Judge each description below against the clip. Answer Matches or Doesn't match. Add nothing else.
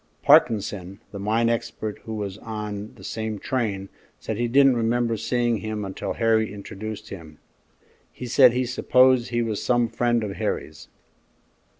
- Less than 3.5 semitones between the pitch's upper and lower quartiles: Matches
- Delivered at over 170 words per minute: Doesn't match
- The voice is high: Doesn't match